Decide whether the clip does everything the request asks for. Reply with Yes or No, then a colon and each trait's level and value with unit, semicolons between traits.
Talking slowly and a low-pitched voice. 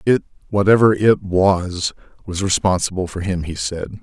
Yes: slow, 120 wpm; very low, 95 Hz